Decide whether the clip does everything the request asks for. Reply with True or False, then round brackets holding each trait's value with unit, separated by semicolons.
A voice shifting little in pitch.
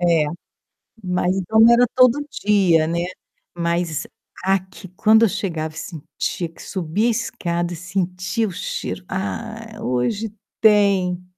False (4.0 semitones)